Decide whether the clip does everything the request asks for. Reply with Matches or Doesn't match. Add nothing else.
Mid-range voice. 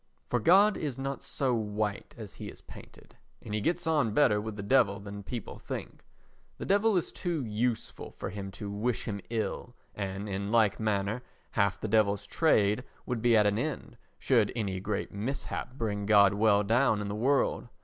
Doesn't match